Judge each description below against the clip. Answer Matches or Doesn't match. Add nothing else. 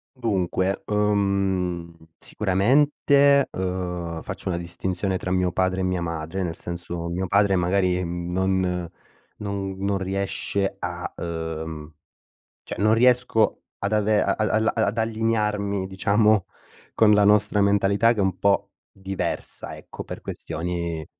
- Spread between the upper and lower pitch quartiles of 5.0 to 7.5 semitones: Doesn't match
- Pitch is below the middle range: Matches